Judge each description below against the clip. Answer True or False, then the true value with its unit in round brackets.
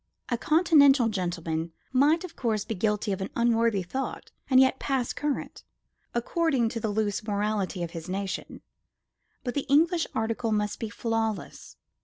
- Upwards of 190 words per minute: False (155 wpm)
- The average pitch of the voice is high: True (225 Hz)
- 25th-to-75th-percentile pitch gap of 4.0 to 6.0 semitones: True (4.6 semitones)